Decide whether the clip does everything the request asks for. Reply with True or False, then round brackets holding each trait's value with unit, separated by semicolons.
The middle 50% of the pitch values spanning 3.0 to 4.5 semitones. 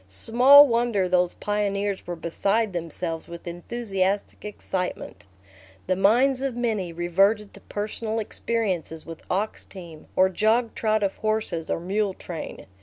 True (4.0 semitones)